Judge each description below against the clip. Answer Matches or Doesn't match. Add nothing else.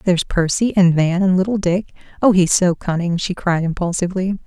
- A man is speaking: Doesn't match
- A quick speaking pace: Doesn't match